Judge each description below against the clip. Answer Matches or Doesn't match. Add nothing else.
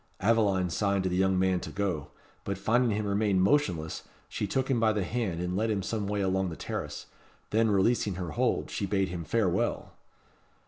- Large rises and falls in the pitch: Doesn't match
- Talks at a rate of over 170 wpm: Matches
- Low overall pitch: Matches